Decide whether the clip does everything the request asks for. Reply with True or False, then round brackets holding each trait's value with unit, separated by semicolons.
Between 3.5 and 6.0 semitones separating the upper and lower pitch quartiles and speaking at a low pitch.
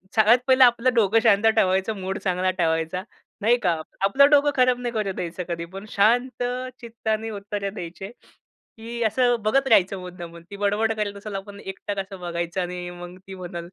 False (3.8 semitones; 200 Hz)